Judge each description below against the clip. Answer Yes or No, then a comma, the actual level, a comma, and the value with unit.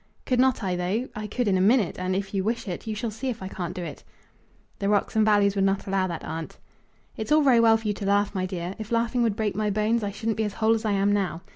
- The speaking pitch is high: Yes, high, 205 Hz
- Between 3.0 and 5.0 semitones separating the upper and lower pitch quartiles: No, narrow, 2.6 semitones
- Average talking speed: No, fast, 290 wpm